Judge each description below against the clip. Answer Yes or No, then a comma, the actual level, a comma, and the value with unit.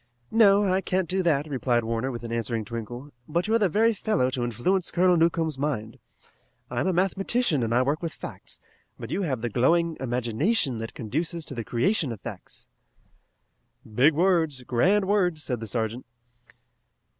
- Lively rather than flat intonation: Yes, wide, 7.3 semitones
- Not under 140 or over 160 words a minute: No, average, 170 wpm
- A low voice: No, medium, 145 Hz